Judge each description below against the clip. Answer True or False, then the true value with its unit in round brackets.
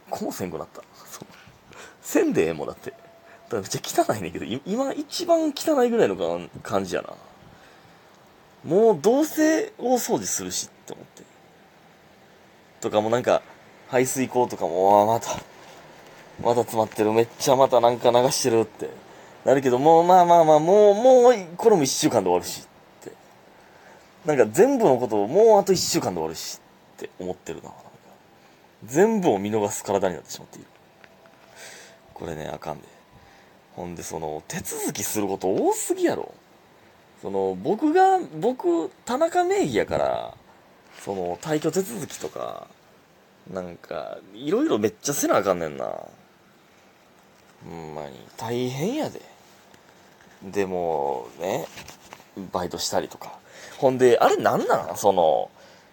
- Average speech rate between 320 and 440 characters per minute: False (275 characters per minute)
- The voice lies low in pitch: True (125 Hz)